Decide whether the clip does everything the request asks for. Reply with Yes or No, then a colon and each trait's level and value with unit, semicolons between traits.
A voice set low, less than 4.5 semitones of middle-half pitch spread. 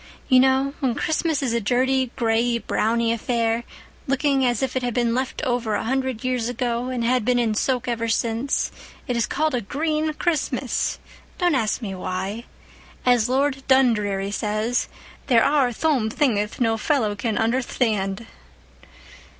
No: high, 245 Hz; average, 2.8 semitones